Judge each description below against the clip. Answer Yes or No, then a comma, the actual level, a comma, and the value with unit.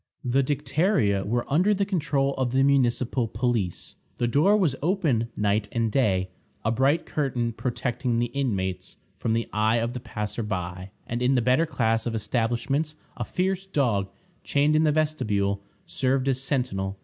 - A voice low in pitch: Yes, low, 125 Hz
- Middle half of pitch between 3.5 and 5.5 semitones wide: Yes, average, 4.3 semitones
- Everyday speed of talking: Yes, average, 165 wpm